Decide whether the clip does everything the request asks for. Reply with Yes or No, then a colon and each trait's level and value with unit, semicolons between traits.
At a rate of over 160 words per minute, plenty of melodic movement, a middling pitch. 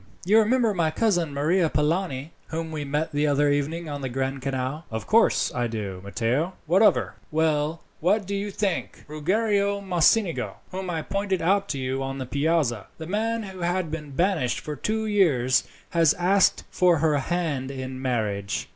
Yes: average, 180 wpm; wide, 5.8 semitones; medium, 160 Hz